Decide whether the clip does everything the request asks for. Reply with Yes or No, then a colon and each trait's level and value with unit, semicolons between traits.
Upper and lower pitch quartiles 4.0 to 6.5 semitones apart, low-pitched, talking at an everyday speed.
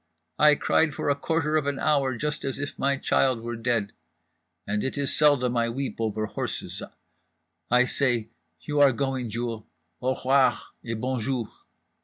No: average, 3.4 semitones; low, 130 Hz; average, 165 wpm